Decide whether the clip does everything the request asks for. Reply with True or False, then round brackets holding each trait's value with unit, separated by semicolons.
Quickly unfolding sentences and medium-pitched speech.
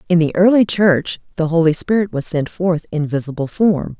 False (195 wpm; 170 Hz)